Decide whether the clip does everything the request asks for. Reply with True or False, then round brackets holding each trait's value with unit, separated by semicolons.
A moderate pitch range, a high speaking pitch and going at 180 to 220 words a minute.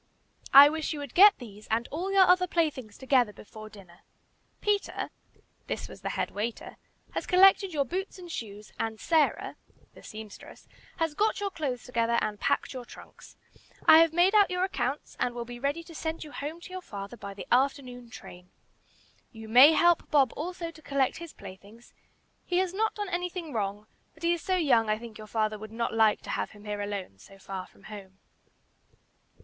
False (7.9 semitones; 265 Hz; 195 wpm)